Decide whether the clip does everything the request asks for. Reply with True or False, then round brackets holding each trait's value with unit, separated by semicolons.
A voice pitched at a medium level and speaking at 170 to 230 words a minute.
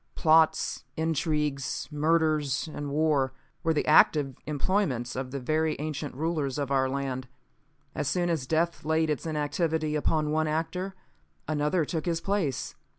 False (155 Hz; 145 wpm)